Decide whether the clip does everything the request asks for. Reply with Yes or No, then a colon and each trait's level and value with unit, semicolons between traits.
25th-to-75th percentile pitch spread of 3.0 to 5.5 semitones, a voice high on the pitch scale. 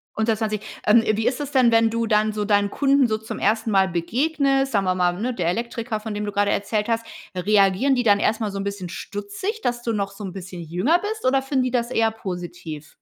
Yes: average, 3.3 semitones; high, 215 Hz